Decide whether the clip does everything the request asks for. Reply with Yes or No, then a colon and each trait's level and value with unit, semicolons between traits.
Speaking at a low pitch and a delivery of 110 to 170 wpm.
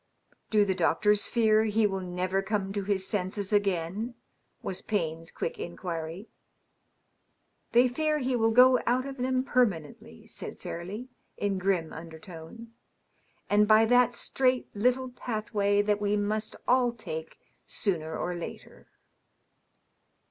No: high, 205 Hz; average, 140 wpm